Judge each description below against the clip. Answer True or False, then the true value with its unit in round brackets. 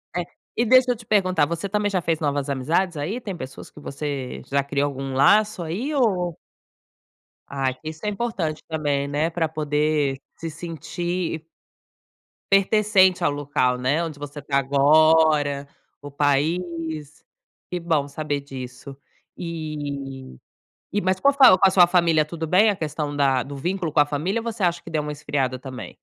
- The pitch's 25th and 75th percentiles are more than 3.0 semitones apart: True (4.1 semitones)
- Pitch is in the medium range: True (155 Hz)